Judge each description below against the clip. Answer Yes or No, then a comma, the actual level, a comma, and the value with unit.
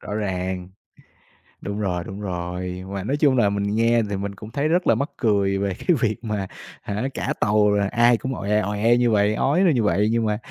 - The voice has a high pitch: No, low, 105 Hz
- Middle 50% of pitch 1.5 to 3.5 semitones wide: Yes, average, 2.9 semitones